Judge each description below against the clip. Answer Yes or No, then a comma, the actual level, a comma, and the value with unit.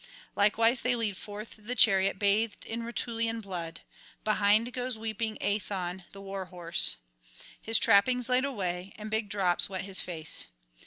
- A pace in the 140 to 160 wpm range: Yes, average, 150 wpm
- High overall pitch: Yes, high, 210 Hz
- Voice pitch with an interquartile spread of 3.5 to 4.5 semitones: No, average, 3.0 semitones